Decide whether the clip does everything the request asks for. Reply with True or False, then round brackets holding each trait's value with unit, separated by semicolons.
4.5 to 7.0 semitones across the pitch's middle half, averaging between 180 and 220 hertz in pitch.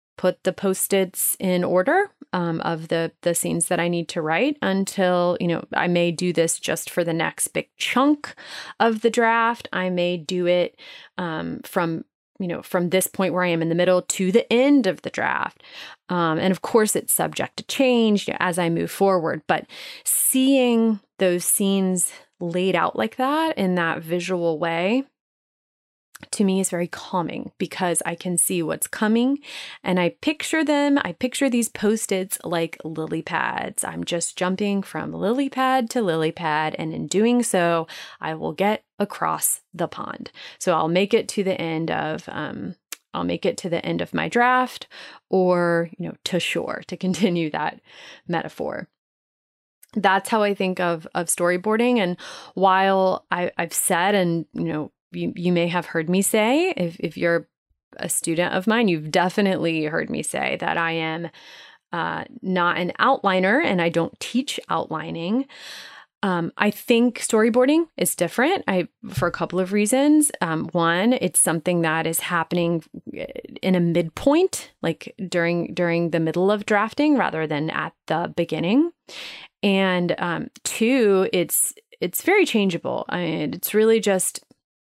True (5.0 semitones; 185 Hz)